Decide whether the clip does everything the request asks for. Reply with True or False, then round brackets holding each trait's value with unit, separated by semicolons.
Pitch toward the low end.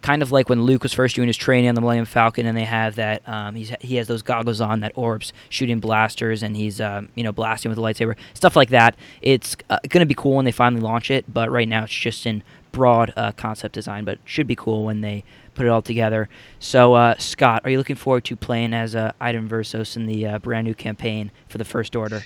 True (115 Hz)